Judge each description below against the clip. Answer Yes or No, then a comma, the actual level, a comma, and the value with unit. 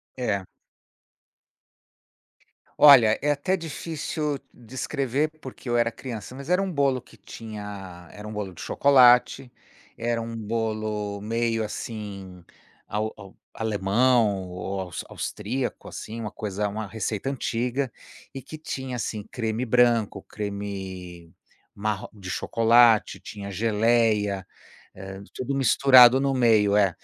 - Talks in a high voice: No, low, 110 Hz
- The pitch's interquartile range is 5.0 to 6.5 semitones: No, average, 3.6 semitones